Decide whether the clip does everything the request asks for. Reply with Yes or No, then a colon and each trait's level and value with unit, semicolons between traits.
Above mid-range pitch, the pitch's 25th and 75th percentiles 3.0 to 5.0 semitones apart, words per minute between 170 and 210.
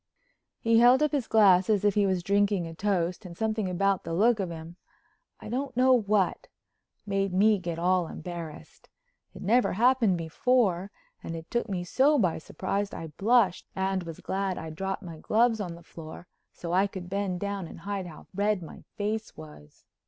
Yes: high, 195 Hz; average, 3.9 semitones; average, 180 wpm